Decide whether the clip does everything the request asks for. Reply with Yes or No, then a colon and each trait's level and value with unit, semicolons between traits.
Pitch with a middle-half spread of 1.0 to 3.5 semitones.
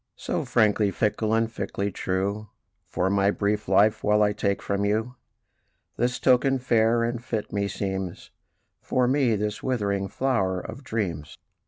Yes: average, 2.7 semitones